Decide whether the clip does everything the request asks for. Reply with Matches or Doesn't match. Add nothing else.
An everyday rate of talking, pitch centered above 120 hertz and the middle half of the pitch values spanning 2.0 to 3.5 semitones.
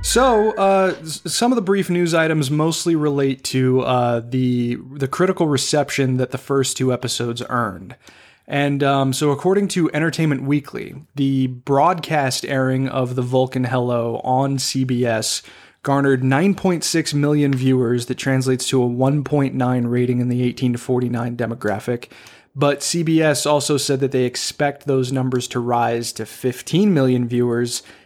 Matches